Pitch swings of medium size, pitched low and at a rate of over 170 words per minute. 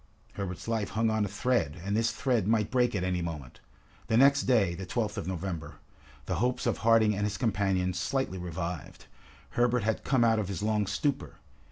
Yes: average, 4.0 semitones; low, 105 Hz; average, 195 wpm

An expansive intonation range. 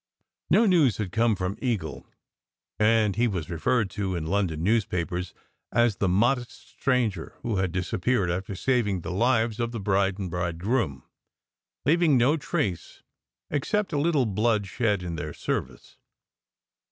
No: average, 4.9 semitones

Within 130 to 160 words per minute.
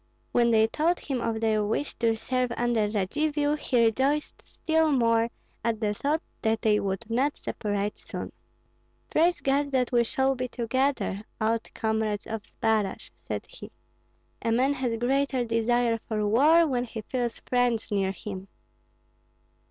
Yes: average, 150 wpm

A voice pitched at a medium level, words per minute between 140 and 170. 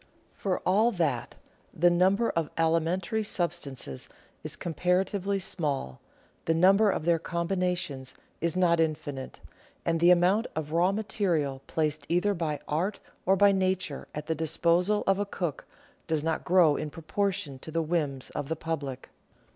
Yes: medium, 170 Hz; average, 155 wpm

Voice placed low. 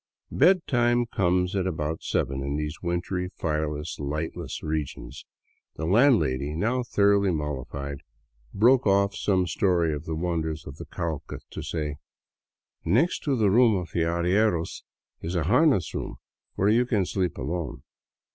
Yes: very low, 85 Hz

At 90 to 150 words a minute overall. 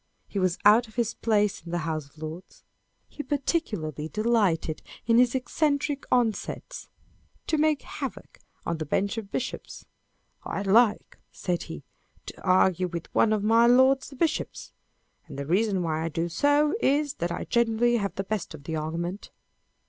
No: average, 170 wpm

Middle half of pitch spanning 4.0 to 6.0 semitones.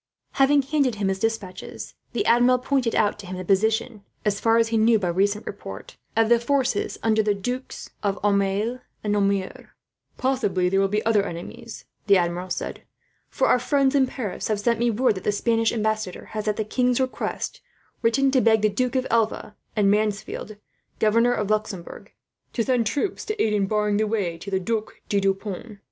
No: average, 2.9 semitones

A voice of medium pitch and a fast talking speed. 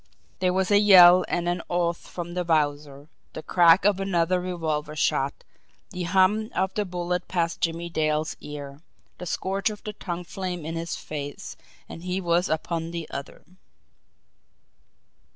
No: medium, 175 Hz; average, 155 wpm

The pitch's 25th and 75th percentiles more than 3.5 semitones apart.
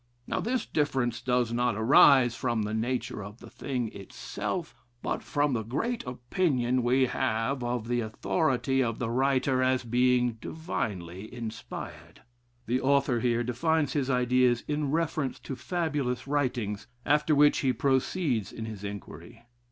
No: average, 3.2 semitones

